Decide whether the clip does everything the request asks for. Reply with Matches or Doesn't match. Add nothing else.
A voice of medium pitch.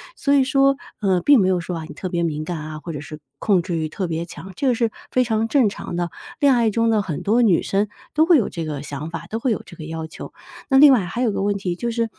Doesn't match